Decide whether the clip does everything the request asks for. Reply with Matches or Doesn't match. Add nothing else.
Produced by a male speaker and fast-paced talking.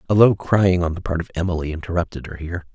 Matches